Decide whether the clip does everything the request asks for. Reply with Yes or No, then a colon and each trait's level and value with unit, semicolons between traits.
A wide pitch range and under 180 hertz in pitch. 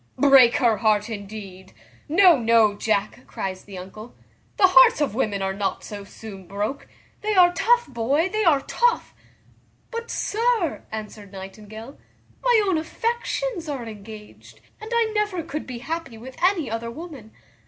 No: wide, 9.0 semitones; very high, 250 Hz